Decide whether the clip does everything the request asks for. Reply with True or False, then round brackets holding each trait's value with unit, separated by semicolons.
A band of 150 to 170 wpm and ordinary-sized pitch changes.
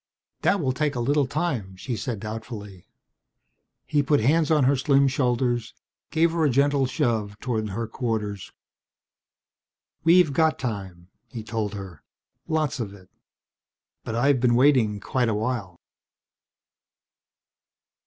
False (135 wpm; 5.0 semitones)